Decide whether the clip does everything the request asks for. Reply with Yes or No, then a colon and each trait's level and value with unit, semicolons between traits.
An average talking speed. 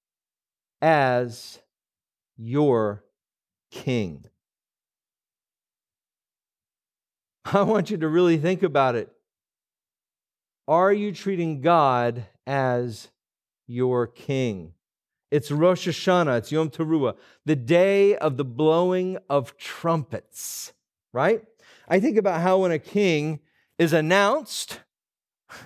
No: slow, 95 wpm